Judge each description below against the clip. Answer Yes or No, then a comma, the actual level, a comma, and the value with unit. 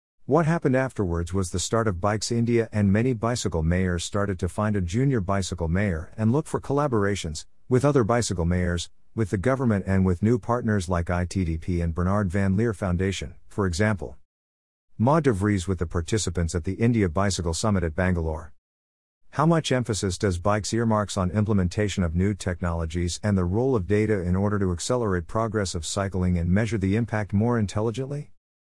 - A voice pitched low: Yes, low, 100 Hz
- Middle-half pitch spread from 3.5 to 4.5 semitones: Yes, average, 4.0 semitones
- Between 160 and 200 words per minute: Yes, average, 180 wpm